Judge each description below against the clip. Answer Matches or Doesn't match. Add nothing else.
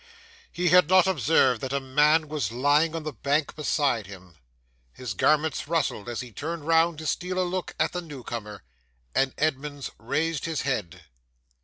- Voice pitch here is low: Doesn't match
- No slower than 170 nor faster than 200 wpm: Matches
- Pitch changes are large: Doesn't match